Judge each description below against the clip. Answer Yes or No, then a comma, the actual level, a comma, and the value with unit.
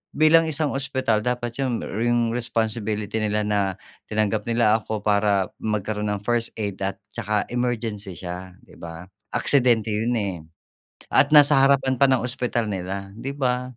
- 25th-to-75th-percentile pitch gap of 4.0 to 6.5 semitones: No, average, 3.2 semitones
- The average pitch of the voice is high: No, low, 110 Hz